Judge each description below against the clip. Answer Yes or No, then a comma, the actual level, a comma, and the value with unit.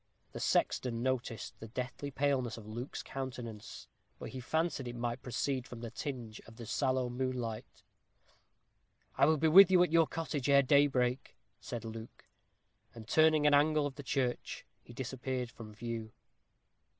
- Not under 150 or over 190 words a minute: Yes, average, 160 wpm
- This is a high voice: No, low, 130 Hz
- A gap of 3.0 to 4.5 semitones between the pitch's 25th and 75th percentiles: Yes, average, 3.3 semitones